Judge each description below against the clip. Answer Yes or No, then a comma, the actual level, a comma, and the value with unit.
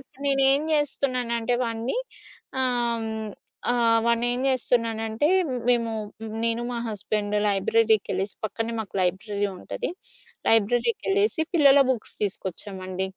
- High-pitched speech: Yes, high, 230 Hz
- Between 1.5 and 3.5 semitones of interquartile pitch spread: Yes, average, 2.8 semitones